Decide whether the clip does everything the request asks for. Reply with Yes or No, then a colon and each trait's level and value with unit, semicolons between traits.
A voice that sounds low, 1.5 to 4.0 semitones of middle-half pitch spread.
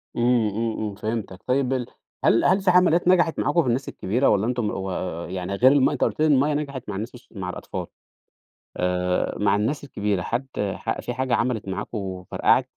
No: low, 115 Hz; wide, 5.4 semitones